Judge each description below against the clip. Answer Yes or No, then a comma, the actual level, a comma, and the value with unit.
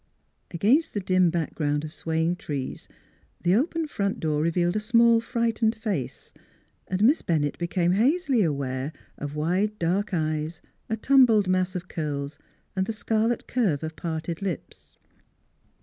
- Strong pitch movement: Yes, wide, 5.7 semitones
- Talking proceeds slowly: No, average, 145 wpm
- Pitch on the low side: No, medium, 185 Hz